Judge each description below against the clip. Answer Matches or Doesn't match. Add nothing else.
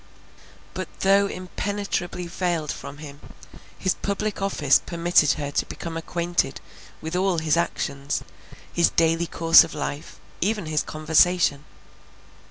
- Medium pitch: Matches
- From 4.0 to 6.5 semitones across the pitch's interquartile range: Doesn't match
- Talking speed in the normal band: Doesn't match